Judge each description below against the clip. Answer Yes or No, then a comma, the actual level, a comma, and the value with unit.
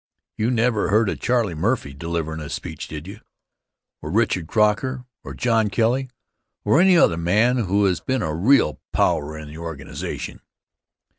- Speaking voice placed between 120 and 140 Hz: No, low, 100 Hz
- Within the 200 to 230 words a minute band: No, average, 160 wpm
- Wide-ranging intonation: Yes, wide, 7.1 semitones